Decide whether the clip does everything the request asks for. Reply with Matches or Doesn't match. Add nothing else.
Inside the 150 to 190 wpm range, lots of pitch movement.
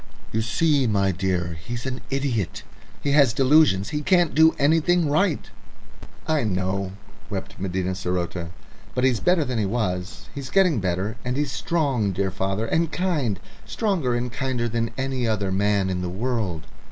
Matches